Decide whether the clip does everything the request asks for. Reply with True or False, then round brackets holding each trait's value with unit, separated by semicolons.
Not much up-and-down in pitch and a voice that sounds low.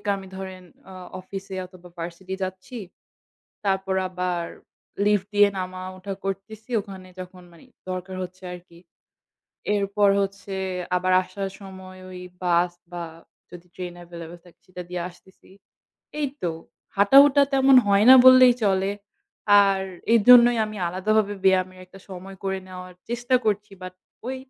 False (1.8 semitones; 190 Hz)